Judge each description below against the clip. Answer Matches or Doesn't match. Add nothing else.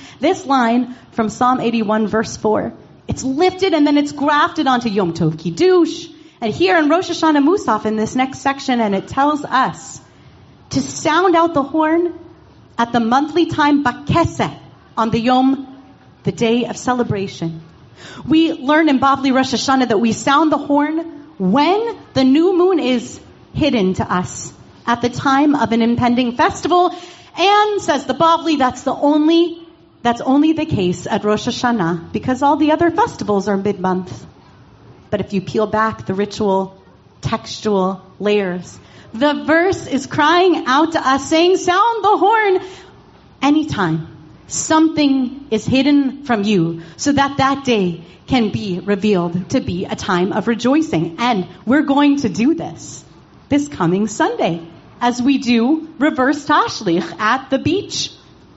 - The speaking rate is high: Doesn't match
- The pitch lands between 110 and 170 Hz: Doesn't match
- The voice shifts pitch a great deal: Matches